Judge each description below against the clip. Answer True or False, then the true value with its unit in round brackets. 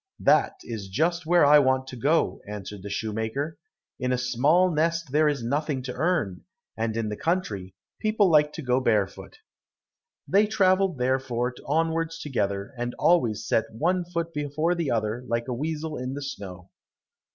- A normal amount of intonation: False (6.1 semitones)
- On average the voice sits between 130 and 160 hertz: True (140 Hz)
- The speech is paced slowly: False (165 wpm)